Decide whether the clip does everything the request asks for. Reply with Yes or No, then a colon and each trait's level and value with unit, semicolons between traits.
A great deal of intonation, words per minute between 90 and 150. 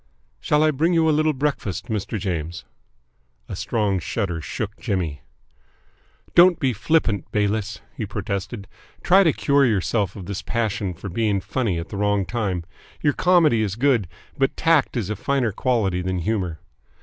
No: wide, 5.9 semitones; average, 160 wpm